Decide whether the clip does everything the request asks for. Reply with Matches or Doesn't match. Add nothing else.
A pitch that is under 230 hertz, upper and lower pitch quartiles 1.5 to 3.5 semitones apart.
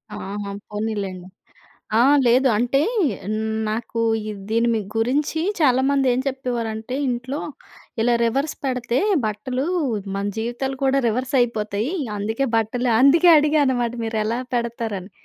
Doesn't match